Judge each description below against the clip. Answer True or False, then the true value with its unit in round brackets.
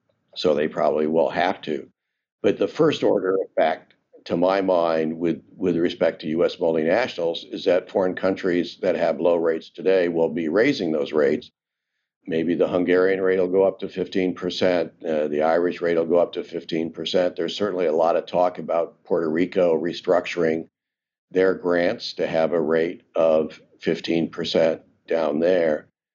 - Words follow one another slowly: False (170 wpm)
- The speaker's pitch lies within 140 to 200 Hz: False (85 Hz)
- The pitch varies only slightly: True (2.1 semitones)